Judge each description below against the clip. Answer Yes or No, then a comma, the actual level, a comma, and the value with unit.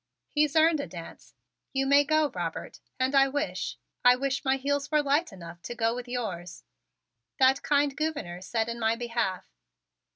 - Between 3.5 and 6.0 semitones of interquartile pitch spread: Yes, average, 4.1 semitones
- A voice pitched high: Yes, very high, 265 Hz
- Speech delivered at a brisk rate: No, average, 170 wpm